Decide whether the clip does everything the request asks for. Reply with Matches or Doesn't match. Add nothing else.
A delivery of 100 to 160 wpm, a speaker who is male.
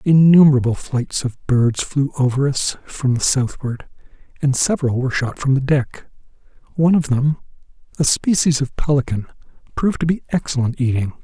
Matches